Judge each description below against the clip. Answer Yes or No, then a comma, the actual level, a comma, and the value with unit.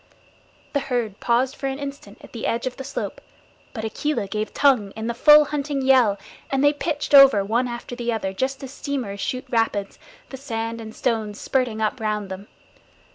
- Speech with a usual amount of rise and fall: Yes, average, 3.8 semitones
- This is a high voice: Yes, high, 240 Hz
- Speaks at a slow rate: No, average, 190 wpm